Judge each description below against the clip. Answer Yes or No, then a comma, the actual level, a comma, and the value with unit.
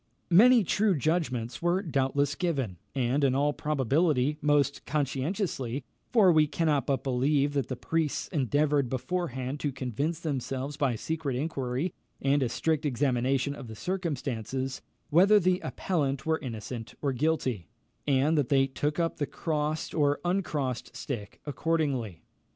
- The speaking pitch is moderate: Yes, medium, 145 Hz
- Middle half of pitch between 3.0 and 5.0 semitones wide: Yes, average, 3.6 semitones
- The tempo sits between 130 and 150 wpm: Yes, average, 140 wpm